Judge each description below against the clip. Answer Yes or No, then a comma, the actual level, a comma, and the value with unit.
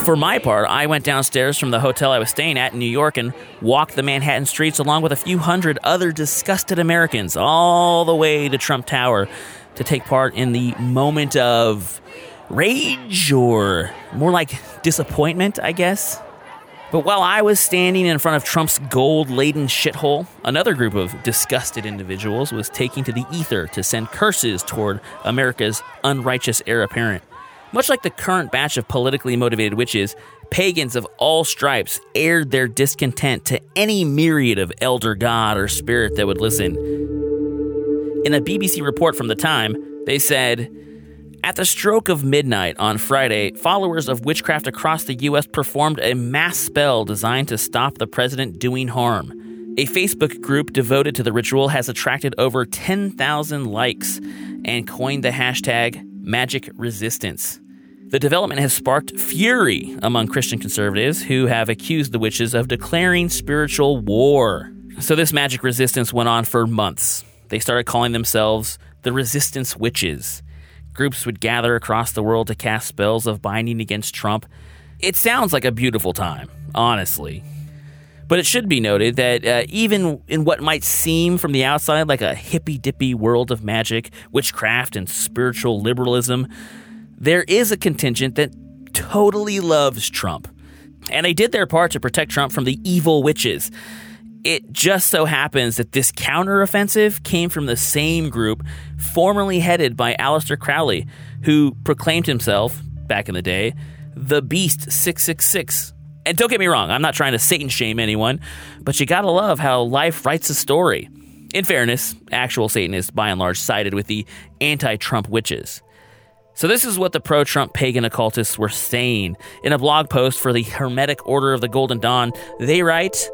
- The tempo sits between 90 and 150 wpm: No, average, 165 wpm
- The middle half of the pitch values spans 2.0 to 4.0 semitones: No, average, 5.1 semitones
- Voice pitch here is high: No, low, 135 Hz